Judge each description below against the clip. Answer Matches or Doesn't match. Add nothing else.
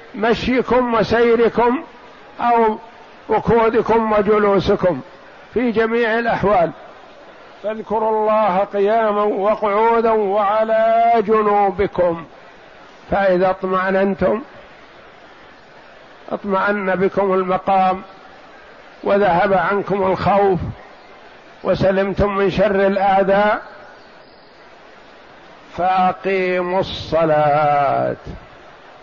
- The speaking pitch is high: Matches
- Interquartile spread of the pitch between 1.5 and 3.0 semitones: Matches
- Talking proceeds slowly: Matches